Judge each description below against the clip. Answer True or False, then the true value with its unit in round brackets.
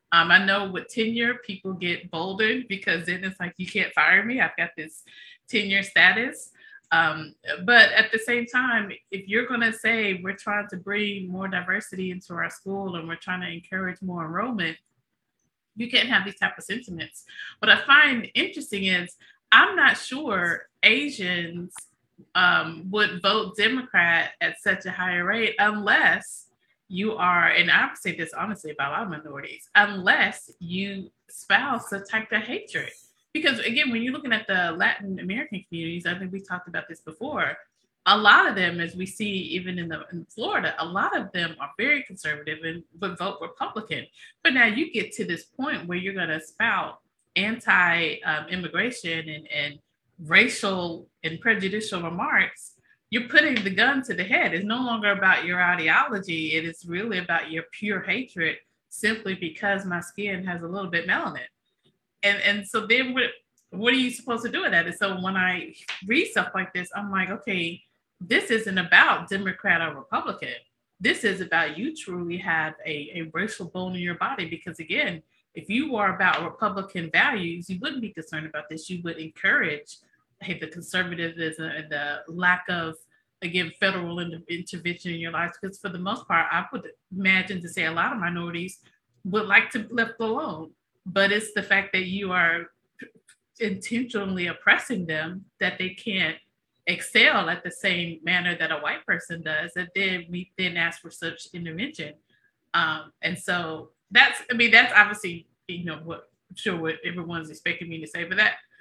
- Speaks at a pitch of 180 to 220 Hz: True (185 Hz)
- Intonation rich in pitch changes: False (3.8 semitones)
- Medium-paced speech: True (180 wpm)